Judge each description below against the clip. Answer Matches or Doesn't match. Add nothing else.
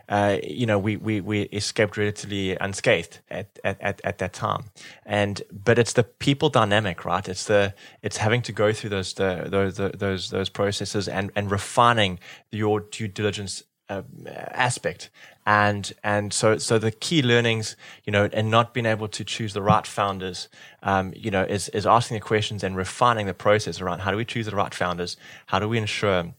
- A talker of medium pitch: Doesn't match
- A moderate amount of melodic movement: Doesn't match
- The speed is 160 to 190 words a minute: Doesn't match